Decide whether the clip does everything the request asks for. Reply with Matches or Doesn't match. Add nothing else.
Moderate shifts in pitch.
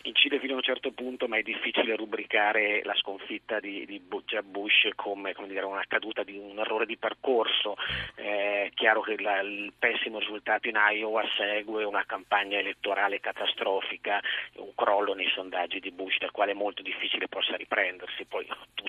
Doesn't match